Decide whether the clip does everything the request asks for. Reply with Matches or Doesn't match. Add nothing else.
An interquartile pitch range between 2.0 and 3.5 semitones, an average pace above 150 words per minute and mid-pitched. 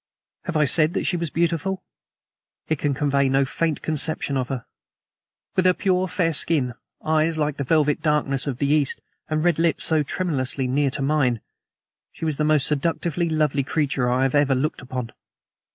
Matches